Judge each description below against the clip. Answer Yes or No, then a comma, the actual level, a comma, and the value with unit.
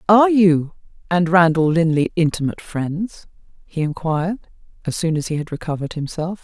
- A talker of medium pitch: Yes, medium, 170 Hz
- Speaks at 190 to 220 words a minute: No, average, 150 wpm